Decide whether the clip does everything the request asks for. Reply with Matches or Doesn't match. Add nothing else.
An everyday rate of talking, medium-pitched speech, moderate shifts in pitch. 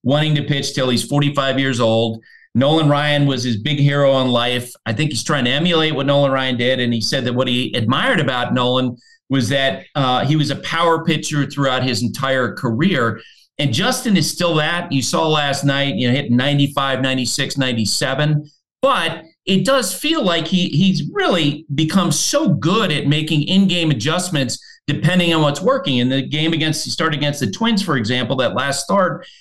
Matches